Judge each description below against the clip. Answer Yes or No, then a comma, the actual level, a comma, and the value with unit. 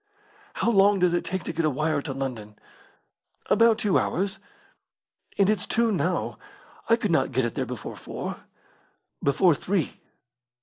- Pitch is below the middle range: No, medium, 180 Hz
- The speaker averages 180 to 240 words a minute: No, average, 160 wpm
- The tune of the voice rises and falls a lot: Yes, wide, 6.1 semitones